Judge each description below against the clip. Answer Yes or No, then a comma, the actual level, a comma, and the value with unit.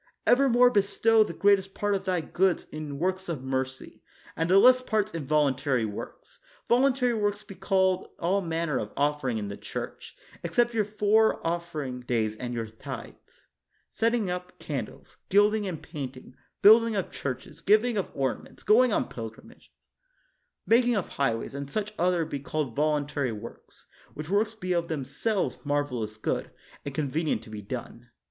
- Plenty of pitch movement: Yes, wide, 7.3 semitones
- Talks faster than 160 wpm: Yes, average, 170 wpm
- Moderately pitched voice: Yes, medium, 170 Hz